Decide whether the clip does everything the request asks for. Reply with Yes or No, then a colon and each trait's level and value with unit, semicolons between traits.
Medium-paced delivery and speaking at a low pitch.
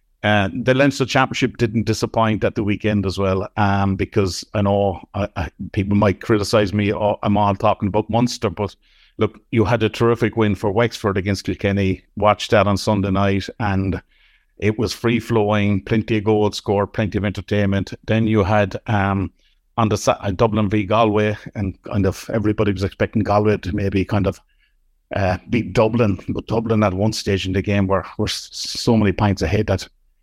Yes: average, 185 wpm; low, 105 Hz